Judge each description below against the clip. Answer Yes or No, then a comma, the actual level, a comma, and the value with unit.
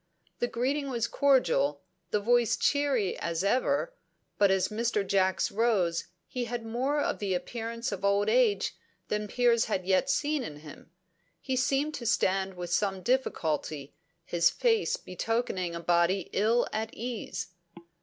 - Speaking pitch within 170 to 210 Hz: No, high, 220 Hz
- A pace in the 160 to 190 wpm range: No, average, 150 wpm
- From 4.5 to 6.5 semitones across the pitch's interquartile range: Yes, average, 5.1 semitones